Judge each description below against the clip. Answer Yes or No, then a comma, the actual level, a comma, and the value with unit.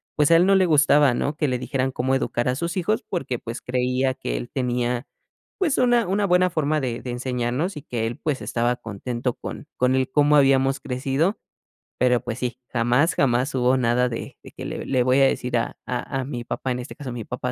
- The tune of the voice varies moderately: Yes, average, 3.3 semitones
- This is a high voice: No, low, 130 Hz